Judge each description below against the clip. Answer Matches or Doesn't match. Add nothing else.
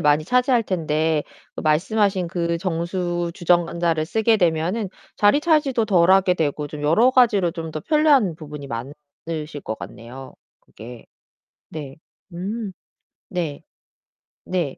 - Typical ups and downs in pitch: Matches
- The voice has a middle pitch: Matches